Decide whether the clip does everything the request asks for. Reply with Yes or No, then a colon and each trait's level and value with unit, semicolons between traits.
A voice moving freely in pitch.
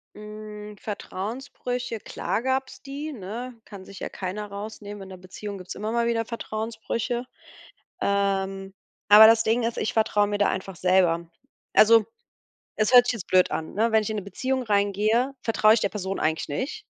No: average, 2.8 semitones